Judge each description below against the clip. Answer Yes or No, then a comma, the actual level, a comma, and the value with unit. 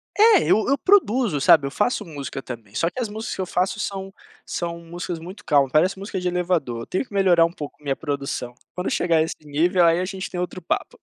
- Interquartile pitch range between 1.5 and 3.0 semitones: No, average, 4.6 semitones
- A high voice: No, medium, 175 Hz